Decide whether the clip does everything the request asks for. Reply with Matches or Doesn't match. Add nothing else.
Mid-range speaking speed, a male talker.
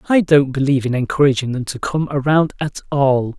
Matches